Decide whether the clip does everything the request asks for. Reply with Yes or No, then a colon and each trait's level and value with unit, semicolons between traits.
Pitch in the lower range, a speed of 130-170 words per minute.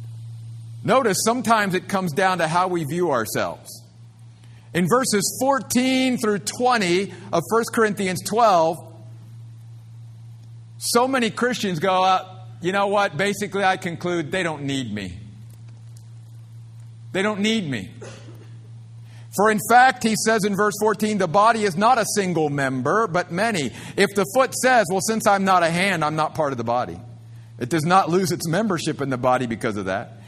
No: medium, 175 Hz; average, 165 wpm